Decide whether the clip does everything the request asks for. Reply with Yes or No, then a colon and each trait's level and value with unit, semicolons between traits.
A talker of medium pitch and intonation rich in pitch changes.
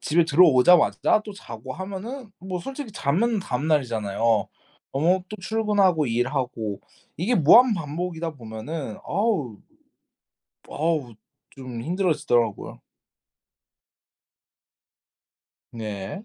Yes: medium, 155 Hz; wide, 7.9 semitones